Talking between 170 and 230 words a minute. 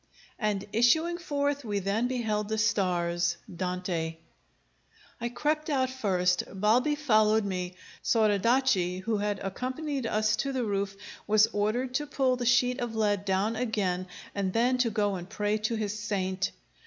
No: average, 155 wpm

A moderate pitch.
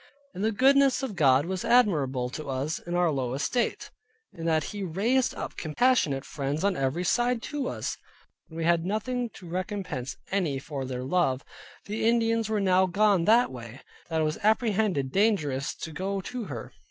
Yes: medium, 180 Hz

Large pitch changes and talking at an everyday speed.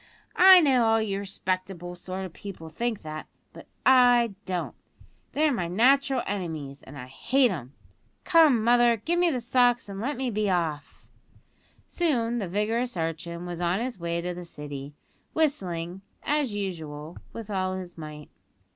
Yes: wide, 6.1 semitones; average, 160 wpm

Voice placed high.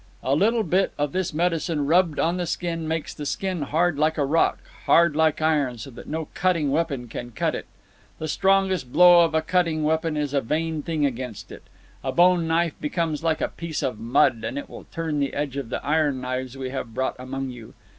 No: medium, 155 Hz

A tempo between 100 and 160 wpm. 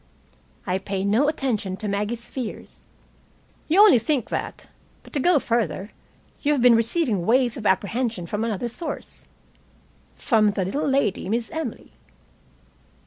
Yes: average, 140 wpm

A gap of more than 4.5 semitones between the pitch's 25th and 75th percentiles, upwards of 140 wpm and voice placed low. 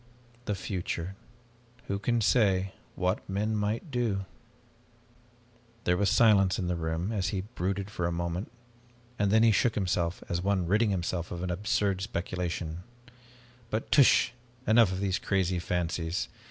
No: average, 3.5 semitones; average, 150 wpm; very low, 95 Hz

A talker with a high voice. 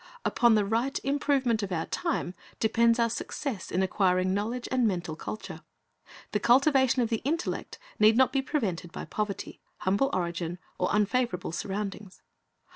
Yes: high, 215 Hz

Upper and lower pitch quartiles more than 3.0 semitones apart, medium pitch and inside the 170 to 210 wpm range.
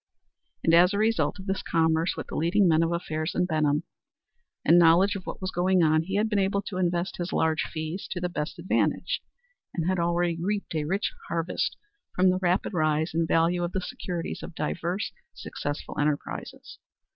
No: narrow, 2.6 semitones; medium, 175 Hz; average, 190 wpm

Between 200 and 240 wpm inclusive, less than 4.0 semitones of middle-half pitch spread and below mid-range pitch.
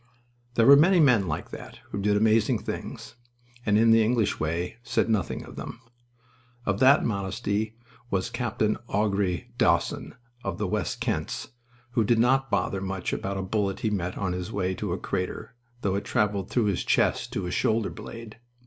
No: average, 180 wpm; average, 2.9 semitones; low, 105 Hz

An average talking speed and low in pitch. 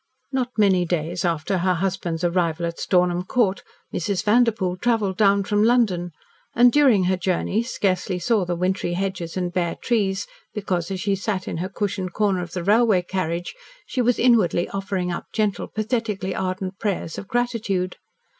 No: average, 165 wpm; high, 190 Hz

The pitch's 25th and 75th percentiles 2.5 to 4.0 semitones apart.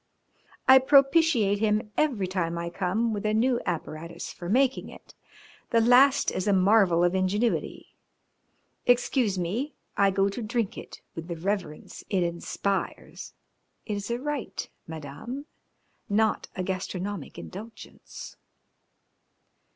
No: average, 4.7 semitones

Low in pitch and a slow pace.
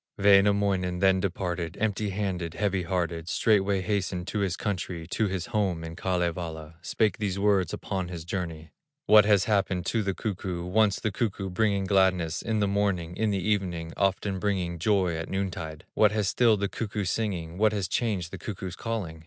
No: very low, 95 Hz; average, 180 wpm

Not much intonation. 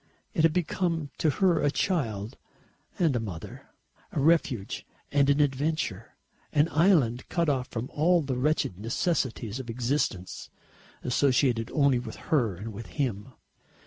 No: average, 5.3 semitones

